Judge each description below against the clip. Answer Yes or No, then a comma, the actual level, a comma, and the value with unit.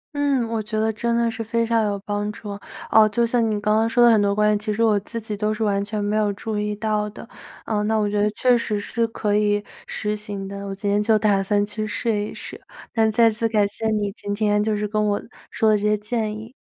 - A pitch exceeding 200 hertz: Yes, high, 210 Hz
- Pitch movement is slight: Yes, narrow, 1.3 semitones